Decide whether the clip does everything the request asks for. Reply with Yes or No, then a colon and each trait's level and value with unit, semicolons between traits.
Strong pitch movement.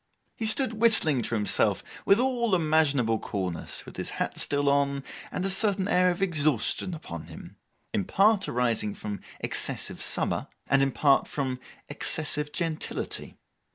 Yes: wide, 7.4 semitones